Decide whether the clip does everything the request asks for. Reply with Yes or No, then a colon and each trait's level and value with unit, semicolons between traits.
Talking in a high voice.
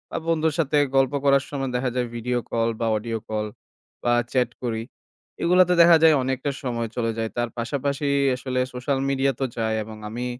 No: low, 125 Hz